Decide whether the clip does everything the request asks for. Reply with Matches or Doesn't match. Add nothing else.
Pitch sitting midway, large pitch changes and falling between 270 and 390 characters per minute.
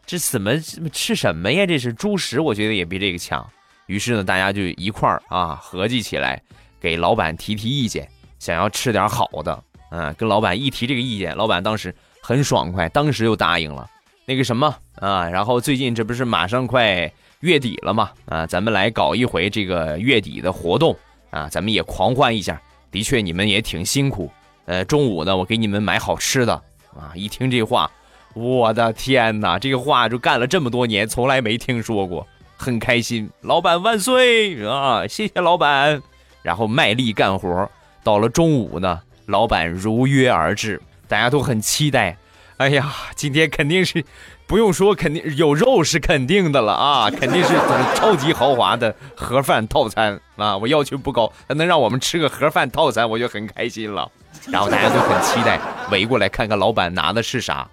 Doesn't match